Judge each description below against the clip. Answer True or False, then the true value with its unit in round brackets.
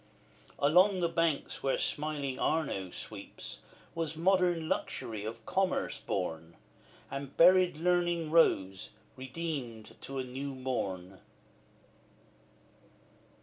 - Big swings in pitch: True (6.3 semitones)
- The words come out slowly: True (100 wpm)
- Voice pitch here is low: False (145 Hz)